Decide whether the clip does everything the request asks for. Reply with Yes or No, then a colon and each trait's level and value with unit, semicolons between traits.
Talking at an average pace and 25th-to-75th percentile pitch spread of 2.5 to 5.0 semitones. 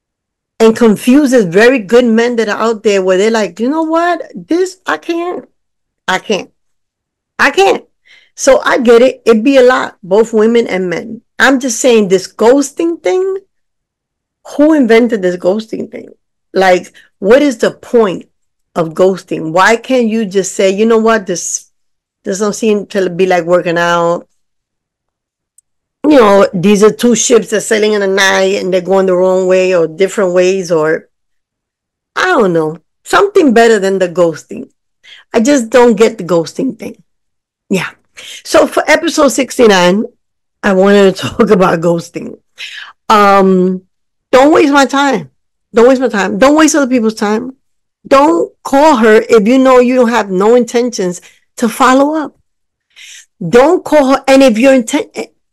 No: average, 165 wpm; wide, 5.6 semitones